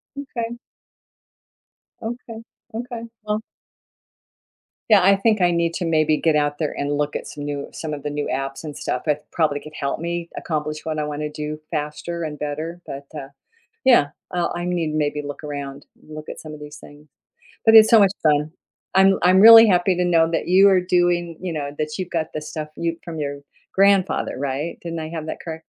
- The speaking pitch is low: No, medium, 160 Hz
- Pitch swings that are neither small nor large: Yes, average, 3.2 semitones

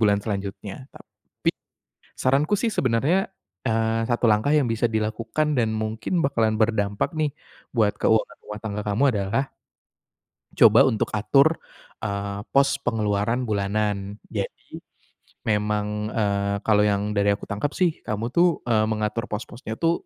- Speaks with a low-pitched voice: Yes, low, 110 Hz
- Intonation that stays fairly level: No, average, 3.3 semitones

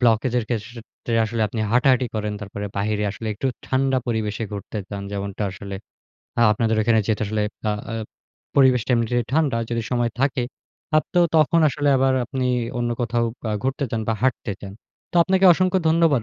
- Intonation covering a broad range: No, average, 3.6 semitones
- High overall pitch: No, low, 120 Hz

